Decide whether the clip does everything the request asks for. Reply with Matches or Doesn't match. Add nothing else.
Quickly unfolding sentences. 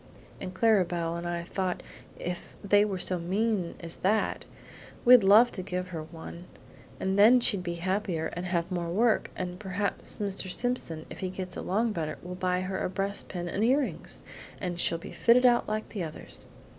Doesn't match